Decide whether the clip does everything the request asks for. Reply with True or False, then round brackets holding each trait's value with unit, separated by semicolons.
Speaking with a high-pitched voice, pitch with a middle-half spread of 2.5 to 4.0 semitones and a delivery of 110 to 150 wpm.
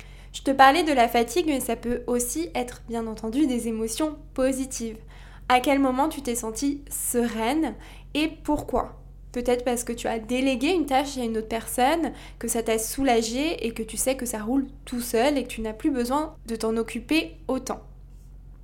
False (245 Hz; 3.1 semitones; 195 wpm)